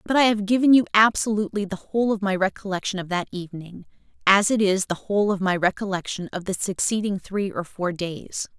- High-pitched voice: Yes, high, 195 Hz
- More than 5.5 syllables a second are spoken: Yes, 5.9 syllables/s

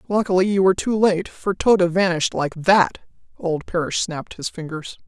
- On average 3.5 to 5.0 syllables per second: No, 5.2 syllables/s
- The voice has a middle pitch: Yes, medium, 180 Hz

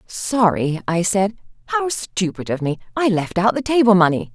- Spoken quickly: No, average, 180 wpm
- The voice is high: Yes, high, 200 Hz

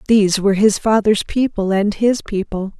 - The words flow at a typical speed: Yes, average, 170 wpm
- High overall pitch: Yes, high, 205 Hz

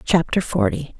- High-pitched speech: No, medium, 155 Hz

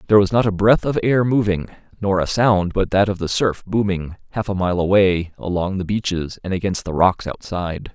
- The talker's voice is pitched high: No, very low, 95 Hz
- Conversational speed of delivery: No, fast, 220 wpm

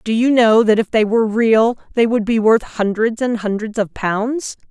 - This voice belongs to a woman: Yes, female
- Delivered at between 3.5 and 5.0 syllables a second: Yes, 4.6 syllables/s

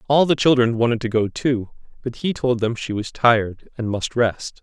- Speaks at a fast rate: Yes, fast, 220 wpm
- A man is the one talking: Yes, male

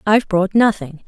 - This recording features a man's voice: No, female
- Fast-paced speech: No, average, 165 wpm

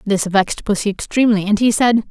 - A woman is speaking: Yes, female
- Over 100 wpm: Yes, average, 200 wpm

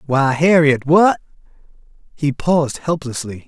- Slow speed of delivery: Yes, slow, 105 wpm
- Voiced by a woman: No, male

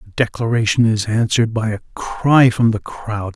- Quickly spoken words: No, average, 180 wpm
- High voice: No, low, 110 Hz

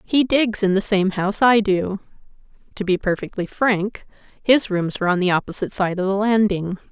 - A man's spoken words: No, female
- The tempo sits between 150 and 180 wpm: No, average, 190 wpm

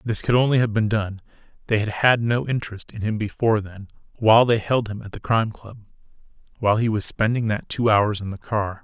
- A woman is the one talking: No, male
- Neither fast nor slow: No, fast, 210 wpm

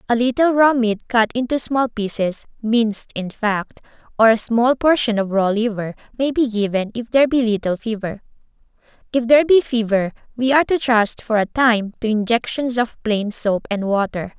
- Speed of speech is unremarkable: Yes, average, 175 wpm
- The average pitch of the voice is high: Yes, high, 230 Hz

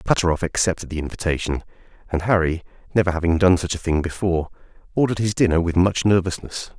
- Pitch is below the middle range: Yes, very low, 85 Hz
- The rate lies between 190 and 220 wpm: No, average, 170 wpm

